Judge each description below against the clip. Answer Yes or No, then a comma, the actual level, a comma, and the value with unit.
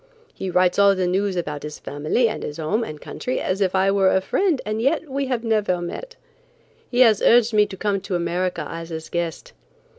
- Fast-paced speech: Yes, fast, 210 wpm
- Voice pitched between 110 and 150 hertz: No, high, 195 Hz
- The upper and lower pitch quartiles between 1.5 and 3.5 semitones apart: No, average, 4.3 semitones